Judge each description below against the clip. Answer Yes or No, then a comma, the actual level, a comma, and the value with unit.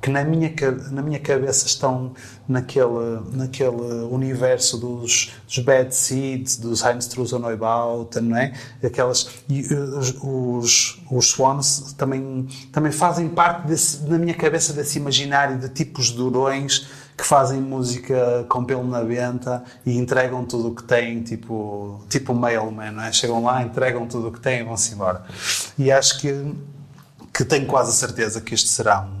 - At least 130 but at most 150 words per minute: No, average, 165 wpm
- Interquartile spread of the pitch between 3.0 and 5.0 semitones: No, narrow, 2.5 semitones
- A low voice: Yes, low, 130 Hz